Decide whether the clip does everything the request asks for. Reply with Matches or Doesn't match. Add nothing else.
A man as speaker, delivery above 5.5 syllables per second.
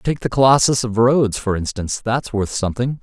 Matches